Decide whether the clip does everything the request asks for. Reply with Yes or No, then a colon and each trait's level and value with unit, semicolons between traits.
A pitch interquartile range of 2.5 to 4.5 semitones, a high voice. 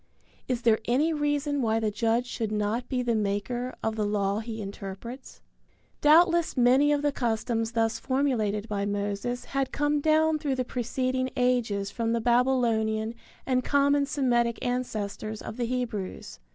Yes: average, 3.4 semitones; high, 240 Hz